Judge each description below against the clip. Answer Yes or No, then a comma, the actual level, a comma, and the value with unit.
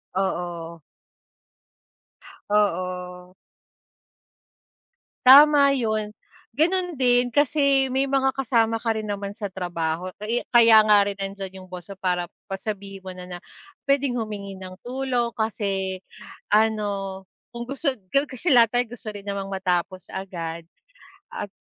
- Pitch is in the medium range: No, high, 205 Hz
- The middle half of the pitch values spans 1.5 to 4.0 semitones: No, average, 4.6 semitones